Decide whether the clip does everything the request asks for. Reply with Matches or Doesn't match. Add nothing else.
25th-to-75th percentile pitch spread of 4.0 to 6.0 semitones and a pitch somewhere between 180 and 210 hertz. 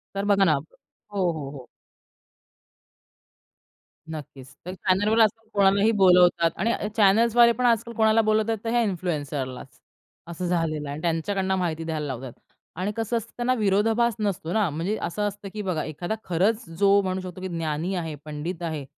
Matches